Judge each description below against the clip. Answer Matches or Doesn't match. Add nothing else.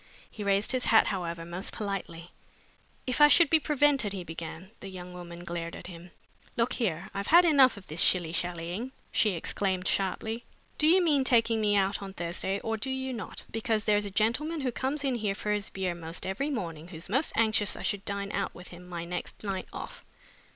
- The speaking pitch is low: Doesn't match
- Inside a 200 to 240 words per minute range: Matches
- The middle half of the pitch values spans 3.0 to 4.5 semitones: Doesn't match